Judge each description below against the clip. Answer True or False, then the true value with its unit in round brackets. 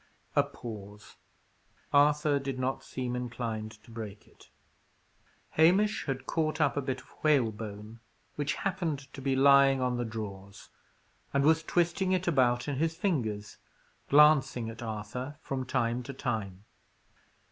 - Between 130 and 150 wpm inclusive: True (140 wpm)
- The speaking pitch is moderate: False (130 Hz)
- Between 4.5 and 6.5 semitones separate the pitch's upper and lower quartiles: True (4.8 semitones)